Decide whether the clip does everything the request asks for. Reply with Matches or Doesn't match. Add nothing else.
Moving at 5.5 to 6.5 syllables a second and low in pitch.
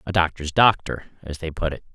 Matches